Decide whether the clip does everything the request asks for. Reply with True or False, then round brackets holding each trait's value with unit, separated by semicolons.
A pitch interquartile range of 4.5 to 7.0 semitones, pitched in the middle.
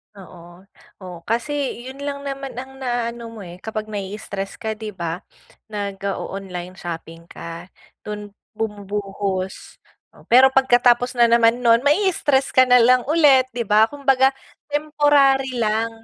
False (5.1 semitones; 230 Hz)